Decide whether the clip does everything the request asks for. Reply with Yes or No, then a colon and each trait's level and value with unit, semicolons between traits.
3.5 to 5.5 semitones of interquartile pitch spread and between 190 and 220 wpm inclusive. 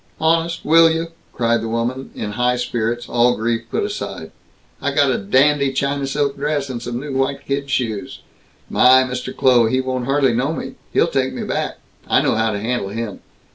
No: average, 3.0 semitones; average, 195 wpm